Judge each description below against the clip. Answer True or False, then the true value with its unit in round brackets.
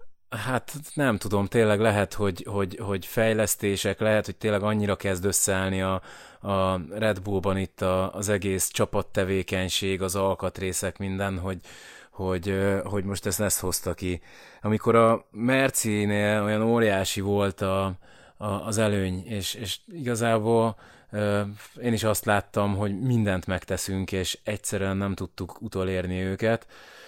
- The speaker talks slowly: False (135 wpm)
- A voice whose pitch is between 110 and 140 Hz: False (100 Hz)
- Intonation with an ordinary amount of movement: False (2.2 semitones)